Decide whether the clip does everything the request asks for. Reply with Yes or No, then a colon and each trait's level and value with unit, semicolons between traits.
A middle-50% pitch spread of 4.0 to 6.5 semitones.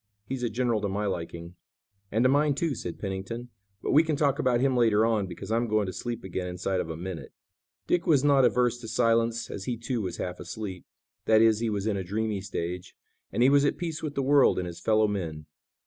Yes: average, 4.8 semitones